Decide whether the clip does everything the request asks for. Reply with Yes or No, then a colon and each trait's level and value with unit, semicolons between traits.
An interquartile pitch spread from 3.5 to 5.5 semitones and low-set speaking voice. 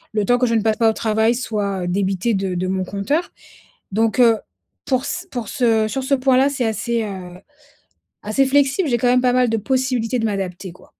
No: average, 4.0 semitones; high, 225 Hz